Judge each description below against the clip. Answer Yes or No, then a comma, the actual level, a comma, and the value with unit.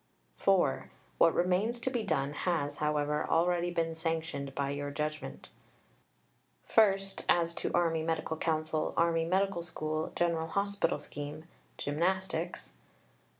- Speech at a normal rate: No, slow, 125 wpm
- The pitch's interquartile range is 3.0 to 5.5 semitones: No, narrow, 2.5 semitones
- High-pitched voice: No, medium, 165 Hz